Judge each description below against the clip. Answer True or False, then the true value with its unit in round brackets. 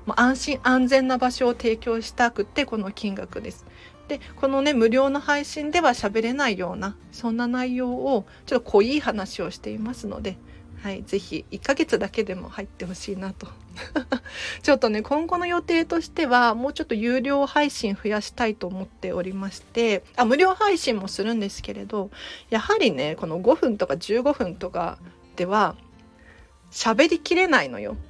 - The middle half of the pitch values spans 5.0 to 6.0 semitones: True (5.5 semitones)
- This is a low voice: False (235 Hz)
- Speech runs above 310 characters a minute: True (320 characters per minute)